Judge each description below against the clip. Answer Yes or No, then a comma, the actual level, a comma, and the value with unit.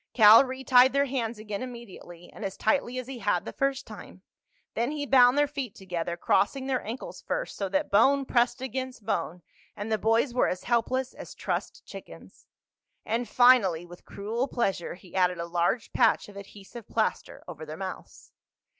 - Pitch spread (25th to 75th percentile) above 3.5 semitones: Yes, average, 5.0 semitones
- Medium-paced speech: Yes, average, 180 wpm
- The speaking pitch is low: No, high, 230 Hz